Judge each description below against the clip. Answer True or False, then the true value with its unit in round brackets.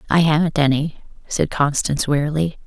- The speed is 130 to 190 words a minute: True (135 wpm)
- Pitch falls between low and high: True (150 Hz)